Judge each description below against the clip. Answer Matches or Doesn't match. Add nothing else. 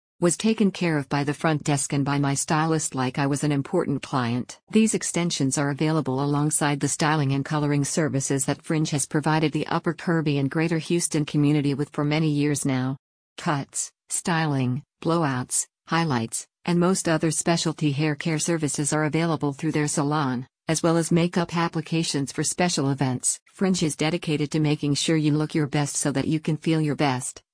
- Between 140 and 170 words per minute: Doesn't match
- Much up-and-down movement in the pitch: Doesn't match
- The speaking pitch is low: Doesn't match